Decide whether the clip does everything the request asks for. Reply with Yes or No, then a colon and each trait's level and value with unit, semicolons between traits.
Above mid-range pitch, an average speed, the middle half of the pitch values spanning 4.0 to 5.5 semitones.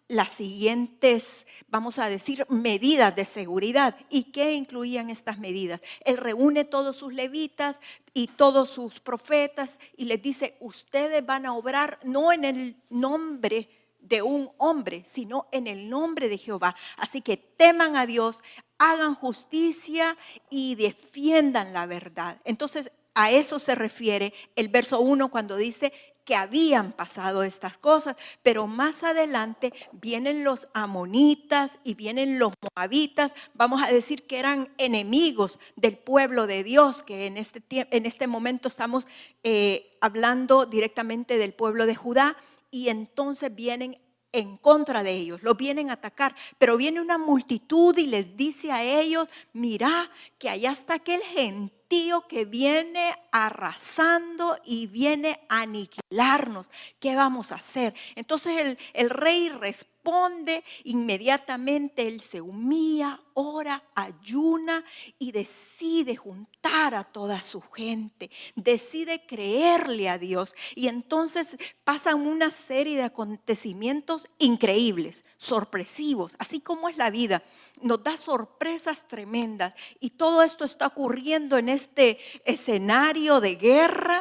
Yes: very high, 260 Hz; average, 135 wpm; average, 4.7 semitones